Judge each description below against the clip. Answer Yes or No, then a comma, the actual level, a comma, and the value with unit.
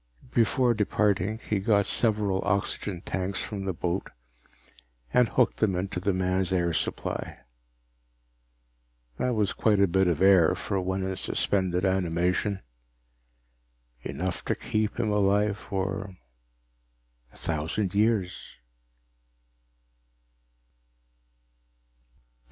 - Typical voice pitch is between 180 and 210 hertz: No, very low, 95 Hz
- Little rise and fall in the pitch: Yes, narrow, 2.2 semitones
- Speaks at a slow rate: Yes, slow, 105 wpm